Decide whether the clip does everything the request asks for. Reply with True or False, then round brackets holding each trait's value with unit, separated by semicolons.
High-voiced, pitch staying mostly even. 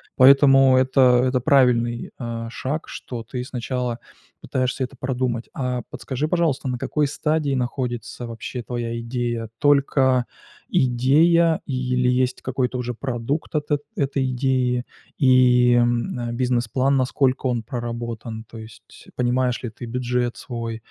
False (125 Hz; 1.9 semitones)